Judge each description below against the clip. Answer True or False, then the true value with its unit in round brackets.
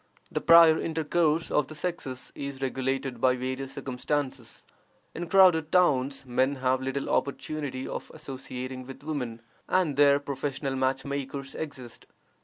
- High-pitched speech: False (140 Hz)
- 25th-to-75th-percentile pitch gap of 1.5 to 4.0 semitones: True (2.7 semitones)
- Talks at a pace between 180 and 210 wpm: False (135 wpm)